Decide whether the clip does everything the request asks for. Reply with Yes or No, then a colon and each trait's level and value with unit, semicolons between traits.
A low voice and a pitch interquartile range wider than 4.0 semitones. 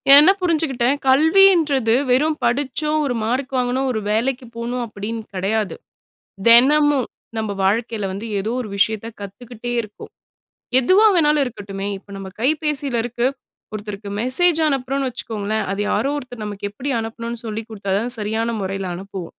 No: high, 235 Hz; average, 4.5 semitones